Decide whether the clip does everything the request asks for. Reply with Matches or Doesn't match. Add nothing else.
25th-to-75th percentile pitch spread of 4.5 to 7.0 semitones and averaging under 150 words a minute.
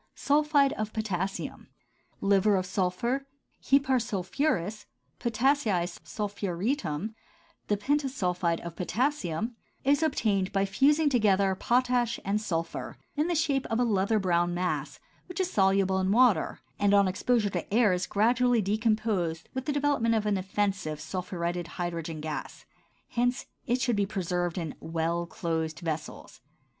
Matches